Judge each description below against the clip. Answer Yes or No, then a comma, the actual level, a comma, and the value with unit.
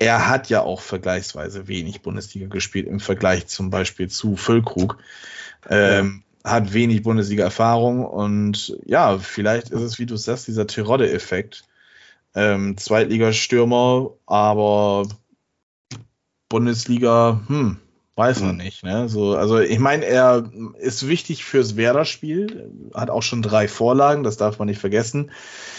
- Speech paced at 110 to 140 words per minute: Yes, average, 130 wpm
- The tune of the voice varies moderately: Yes, average, 3.1 semitones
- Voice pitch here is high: No, low, 110 Hz